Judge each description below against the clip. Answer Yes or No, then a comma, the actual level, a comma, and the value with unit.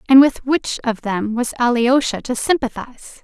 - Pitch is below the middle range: No, very high, 250 Hz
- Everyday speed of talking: Yes, average, 165 wpm